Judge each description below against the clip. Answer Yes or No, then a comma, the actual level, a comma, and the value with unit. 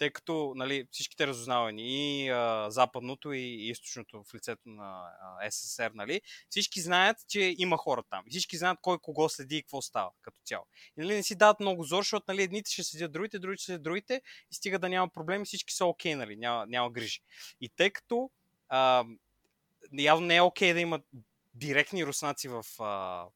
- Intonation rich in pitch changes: Yes, wide, 6.9 semitones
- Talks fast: Yes, fast, 200 wpm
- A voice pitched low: No, medium, 155 Hz